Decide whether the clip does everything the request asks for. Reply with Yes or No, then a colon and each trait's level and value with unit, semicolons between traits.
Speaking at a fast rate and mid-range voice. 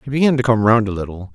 No: fast, 310 wpm; low, 115 Hz